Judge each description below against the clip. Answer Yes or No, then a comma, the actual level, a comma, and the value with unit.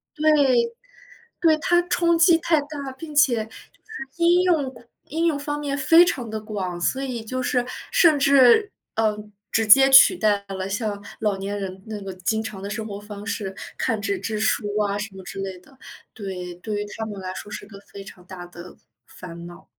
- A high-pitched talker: Yes, high, 220 Hz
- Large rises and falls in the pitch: Yes, wide, 6.2 semitones